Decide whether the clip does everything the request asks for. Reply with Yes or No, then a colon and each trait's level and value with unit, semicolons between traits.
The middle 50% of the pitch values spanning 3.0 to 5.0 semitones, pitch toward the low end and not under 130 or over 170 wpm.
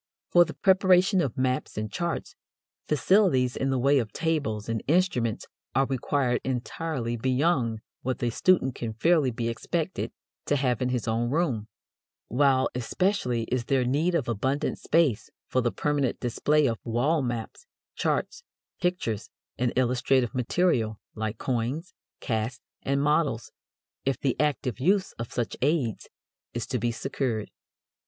Yes: average, 4.3 semitones; low, 130 Hz; average, 145 wpm